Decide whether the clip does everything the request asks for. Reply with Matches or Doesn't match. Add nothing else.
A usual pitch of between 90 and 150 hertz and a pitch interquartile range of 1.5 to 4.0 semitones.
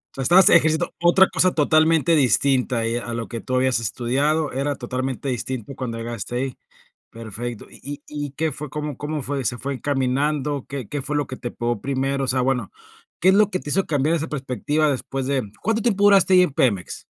Matches